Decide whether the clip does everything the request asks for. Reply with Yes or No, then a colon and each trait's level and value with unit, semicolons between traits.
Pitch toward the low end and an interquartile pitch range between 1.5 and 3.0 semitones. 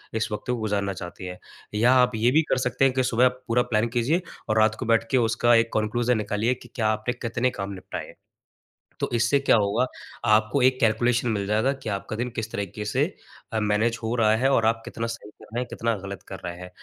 Yes: low, 115 Hz; narrow, 2.5 semitones